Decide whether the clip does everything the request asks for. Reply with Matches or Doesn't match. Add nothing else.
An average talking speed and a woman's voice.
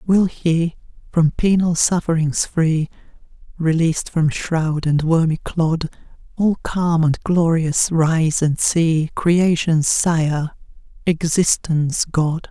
Doesn't match